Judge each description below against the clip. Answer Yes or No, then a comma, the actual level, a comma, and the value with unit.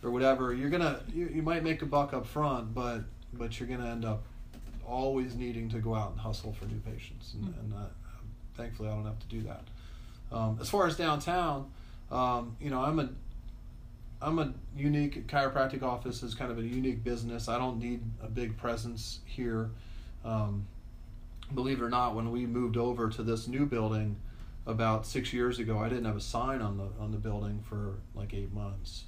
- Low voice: Yes, low, 115 Hz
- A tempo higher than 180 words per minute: Yes, fast, 205 wpm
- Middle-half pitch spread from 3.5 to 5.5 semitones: No, narrow, 2.6 semitones